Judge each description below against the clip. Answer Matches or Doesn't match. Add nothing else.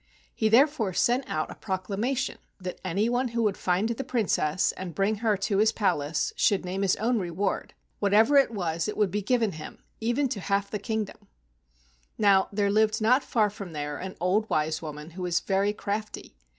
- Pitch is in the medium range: Doesn't match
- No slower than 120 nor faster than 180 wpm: Doesn't match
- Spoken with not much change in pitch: Doesn't match